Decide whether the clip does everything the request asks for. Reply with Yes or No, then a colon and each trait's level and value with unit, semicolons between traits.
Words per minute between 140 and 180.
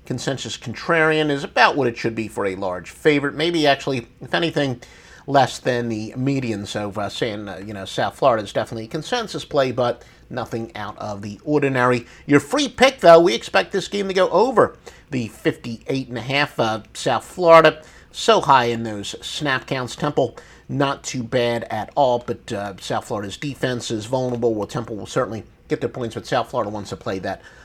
No: average, 190 wpm